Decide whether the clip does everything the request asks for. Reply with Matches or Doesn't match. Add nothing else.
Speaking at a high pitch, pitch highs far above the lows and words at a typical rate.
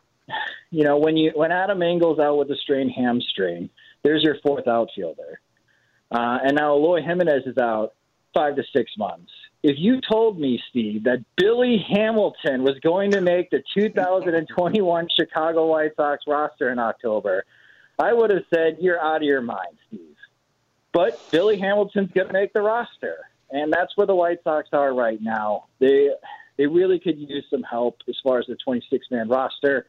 Doesn't match